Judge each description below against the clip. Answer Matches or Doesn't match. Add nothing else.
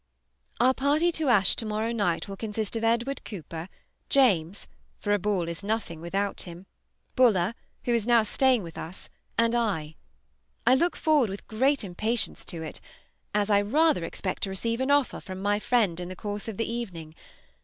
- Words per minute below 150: Doesn't match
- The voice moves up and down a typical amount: Matches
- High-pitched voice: Matches